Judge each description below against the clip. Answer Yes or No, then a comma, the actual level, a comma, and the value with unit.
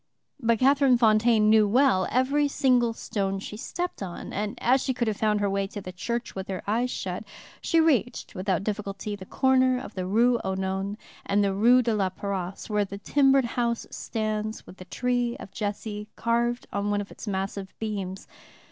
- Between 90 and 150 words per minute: No, average, 190 wpm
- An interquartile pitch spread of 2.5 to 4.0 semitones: Yes, average, 3.6 semitones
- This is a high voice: Yes, high, 215 Hz